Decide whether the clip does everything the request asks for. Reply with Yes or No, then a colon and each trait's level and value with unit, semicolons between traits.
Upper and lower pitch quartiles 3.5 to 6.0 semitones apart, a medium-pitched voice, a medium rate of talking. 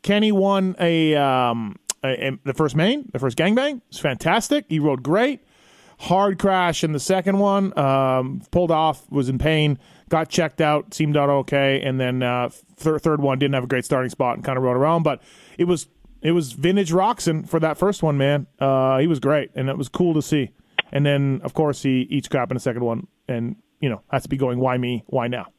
No: average, 4.4 semitones; medium, 150 Hz; fast, 225 wpm